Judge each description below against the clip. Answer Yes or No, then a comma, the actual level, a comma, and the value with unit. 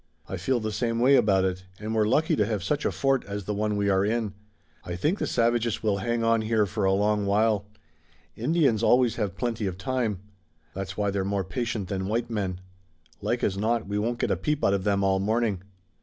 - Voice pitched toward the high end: No, low, 105 Hz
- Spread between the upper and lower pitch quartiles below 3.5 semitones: Yes, average, 3.0 semitones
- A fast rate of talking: Yes, fast, 230 wpm